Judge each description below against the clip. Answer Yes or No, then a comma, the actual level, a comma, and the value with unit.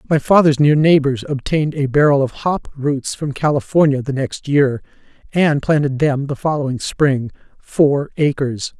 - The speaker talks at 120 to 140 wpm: No, average, 150 wpm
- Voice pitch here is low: No, medium, 145 Hz